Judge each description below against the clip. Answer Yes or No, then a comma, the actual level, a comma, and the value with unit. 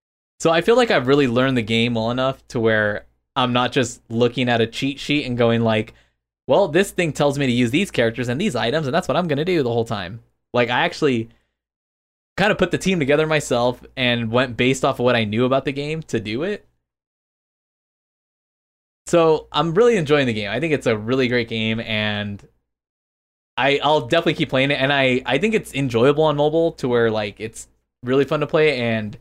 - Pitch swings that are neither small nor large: Yes, average, 4.9 semitones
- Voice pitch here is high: No, low, 125 Hz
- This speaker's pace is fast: Yes, fast, 220 wpm